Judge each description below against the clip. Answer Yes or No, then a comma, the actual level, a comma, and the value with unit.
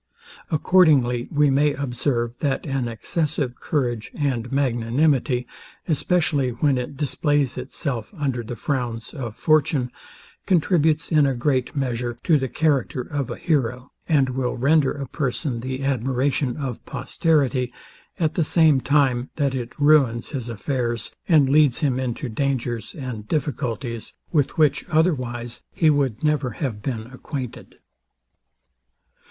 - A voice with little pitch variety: No, average, 3.4 semitones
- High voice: No, low, 135 Hz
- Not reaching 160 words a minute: Yes, slow, 135 wpm